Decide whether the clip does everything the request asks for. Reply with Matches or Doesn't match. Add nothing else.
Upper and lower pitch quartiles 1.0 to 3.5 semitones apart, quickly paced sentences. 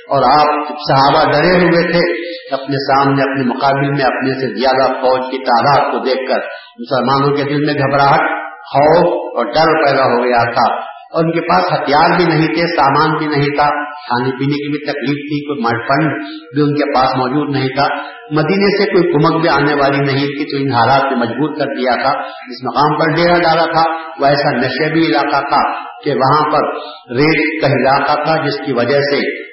Matches